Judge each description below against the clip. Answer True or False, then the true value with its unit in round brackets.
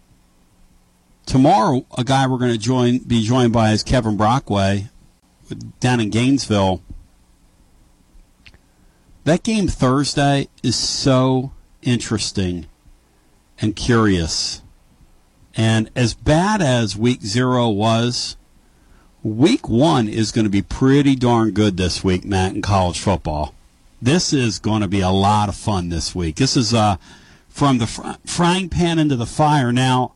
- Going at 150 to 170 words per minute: False (135 wpm)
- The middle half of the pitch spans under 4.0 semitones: False (5.2 semitones)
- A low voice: True (110 Hz)